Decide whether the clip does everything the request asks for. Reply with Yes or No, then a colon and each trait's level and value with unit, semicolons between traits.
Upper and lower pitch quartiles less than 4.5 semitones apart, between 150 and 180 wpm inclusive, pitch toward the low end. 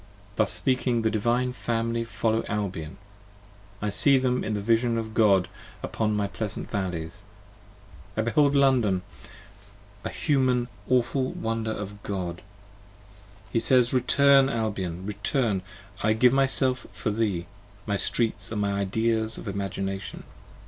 No: average, 3.7 semitones; slow, 135 wpm; low, 110 Hz